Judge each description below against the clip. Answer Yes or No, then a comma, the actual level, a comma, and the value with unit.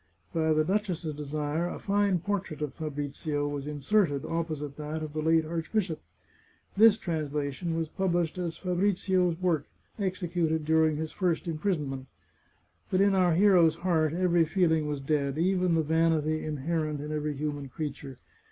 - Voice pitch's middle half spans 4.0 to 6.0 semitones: No, average, 3.0 semitones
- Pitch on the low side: No, medium, 160 Hz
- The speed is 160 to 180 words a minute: No, average, 150 wpm